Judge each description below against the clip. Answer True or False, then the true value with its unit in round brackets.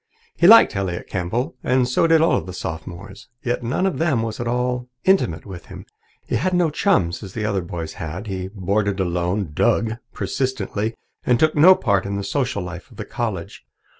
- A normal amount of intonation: False (5.7 semitones)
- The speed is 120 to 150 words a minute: False (195 wpm)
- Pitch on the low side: True (105 Hz)